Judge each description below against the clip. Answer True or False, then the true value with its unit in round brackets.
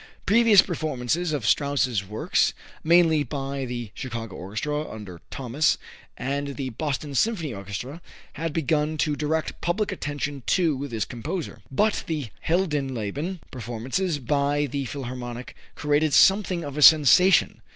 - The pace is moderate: False (130 wpm)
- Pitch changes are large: False (4.2 semitones)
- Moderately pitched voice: True (145 Hz)